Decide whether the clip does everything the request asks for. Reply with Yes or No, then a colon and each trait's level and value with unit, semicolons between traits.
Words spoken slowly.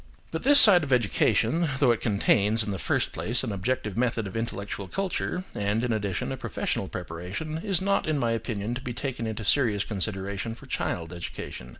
No: average, 195 wpm